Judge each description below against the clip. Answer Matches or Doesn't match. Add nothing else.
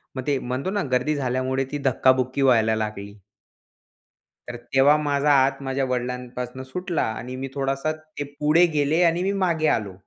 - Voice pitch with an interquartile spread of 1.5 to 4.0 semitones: Matches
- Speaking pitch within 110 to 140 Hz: Matches